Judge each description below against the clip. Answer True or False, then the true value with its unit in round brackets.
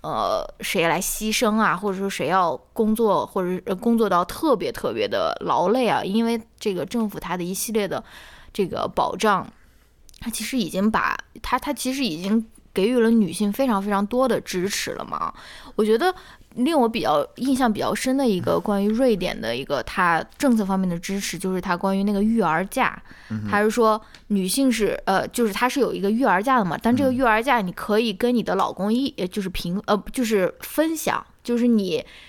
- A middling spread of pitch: True (3.8 semitones)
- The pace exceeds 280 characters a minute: True (290 characters per minute)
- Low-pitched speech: False (220 Hz)